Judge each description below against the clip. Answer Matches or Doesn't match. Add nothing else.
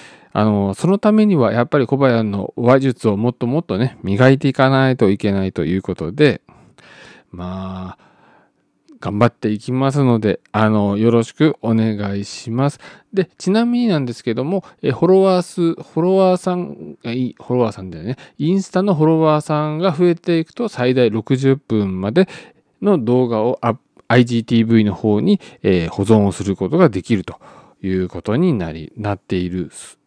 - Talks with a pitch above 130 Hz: Doesn't match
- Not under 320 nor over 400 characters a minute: Matches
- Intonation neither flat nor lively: Doesn't match